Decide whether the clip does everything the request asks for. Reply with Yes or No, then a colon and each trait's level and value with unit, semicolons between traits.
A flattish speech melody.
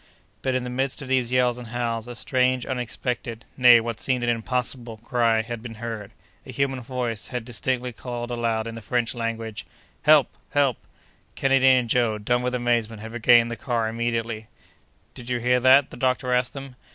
Yes: narrow, 1.7 semitones